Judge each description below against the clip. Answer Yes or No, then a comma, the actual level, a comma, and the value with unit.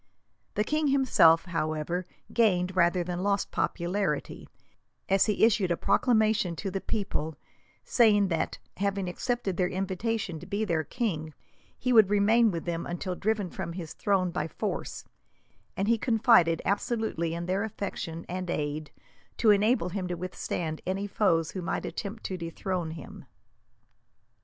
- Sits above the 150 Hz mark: Yes, medium, 185 Hz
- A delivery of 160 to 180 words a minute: No, average, 150 wpm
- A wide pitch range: No, average, 3.8 semitones